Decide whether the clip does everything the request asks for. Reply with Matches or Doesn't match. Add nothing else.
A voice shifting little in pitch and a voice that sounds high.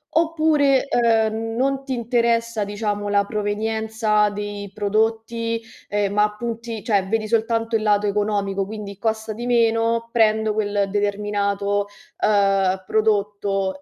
Matches